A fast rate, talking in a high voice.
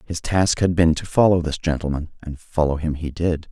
No: fast, 220 wpm; very low, 80 Hz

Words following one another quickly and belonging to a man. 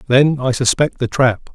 No: average, 195 wpm; male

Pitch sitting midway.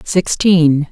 Yes: medium, 165 Hz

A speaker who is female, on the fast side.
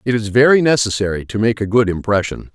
No: male; fast, 210 wpm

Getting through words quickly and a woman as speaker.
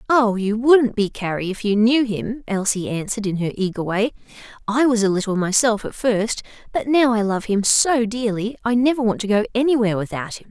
Yes: fast, 210 wpm; female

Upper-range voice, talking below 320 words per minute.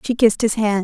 Yes: high, 215 Hz; fast, 285 wpm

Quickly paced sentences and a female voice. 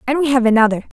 Yes: fast, 240 wpm; female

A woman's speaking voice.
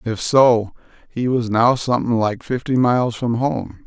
No: male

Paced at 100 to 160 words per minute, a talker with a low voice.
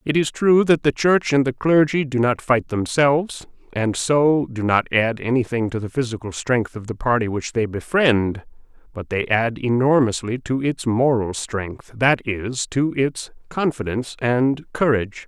No: average, 175 wpm; low, 125 Hz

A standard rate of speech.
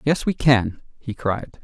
Yes: average, 185 wpm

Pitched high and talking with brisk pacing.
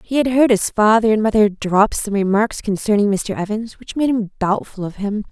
Yes: high, 215 Hz; fast, 215 wpm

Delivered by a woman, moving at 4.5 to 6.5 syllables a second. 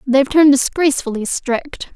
Yes: female; 5.6 syllables/s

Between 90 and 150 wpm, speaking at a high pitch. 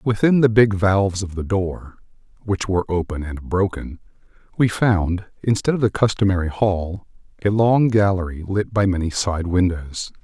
No: average, 145 wpm; very low, 95 Hz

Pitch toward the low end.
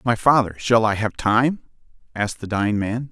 Yes: low, 115 Hz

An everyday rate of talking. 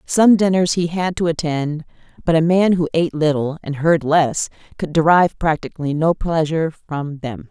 Yes: average, 175 wpm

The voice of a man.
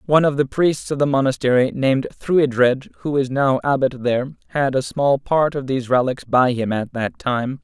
Yes: male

